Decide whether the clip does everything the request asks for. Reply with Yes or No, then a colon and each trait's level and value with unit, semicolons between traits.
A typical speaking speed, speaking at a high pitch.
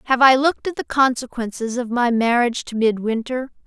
Yes: average, 180 wpm; high, 245 Hz